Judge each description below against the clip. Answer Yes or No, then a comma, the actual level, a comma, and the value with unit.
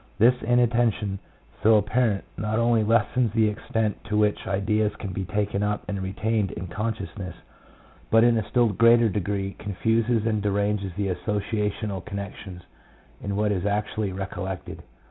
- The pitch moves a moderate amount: No, narrow, 2.2 semitones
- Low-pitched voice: Yes, low, 105 Hz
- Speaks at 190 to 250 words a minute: No, average, 155 wpm